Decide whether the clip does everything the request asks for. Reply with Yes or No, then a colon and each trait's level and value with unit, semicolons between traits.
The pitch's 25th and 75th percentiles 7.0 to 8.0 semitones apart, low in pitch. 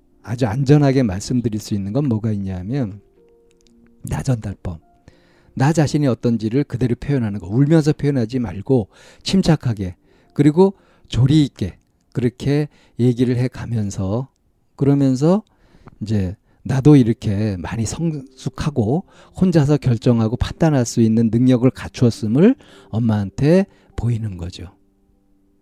No: average, 5.1 semitones; low, 120 Hz